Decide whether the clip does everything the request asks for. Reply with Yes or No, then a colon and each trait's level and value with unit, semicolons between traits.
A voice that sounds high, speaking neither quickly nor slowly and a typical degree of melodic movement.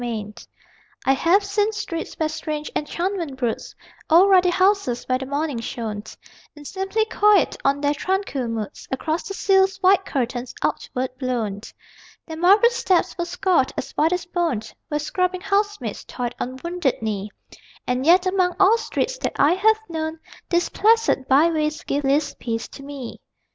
No: very high, 320 Hz; average, 160 wpm; wide, 6.5 semitones